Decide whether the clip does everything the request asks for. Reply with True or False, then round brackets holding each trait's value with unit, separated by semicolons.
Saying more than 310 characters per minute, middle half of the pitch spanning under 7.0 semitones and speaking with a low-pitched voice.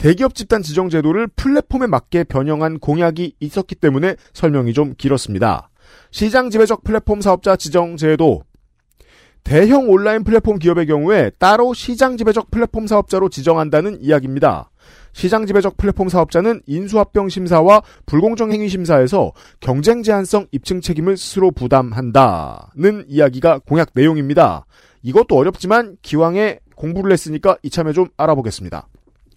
False (360 characters per minute; 5.6 semitones; 180 Hz)